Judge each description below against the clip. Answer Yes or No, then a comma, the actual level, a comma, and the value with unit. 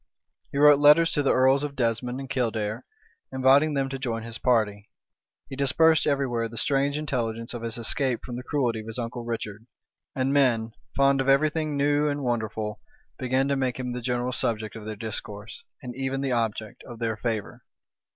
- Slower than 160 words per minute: No, average, 195 wpm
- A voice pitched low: Yes, low, 125 Hz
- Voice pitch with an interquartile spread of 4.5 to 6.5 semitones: No, average, 3.3 semitones